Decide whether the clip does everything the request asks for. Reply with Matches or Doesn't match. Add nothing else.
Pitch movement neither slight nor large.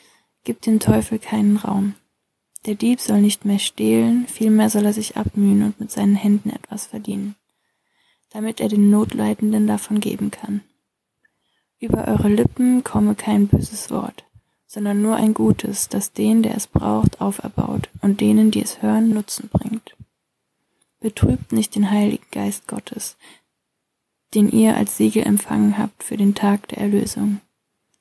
Doesn't match